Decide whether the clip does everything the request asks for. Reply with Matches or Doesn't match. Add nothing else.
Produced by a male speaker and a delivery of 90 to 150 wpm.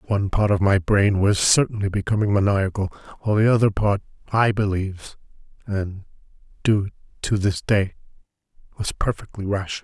Matches